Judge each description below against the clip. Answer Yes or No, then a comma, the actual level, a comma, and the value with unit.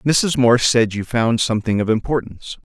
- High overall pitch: No, low, 120 Hz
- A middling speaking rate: Yes, average, 180 wpm